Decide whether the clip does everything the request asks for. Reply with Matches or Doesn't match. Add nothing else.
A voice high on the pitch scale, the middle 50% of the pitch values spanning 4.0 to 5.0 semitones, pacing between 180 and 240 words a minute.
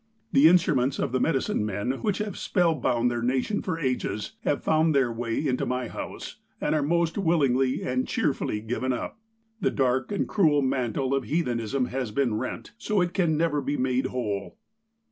Doesn't match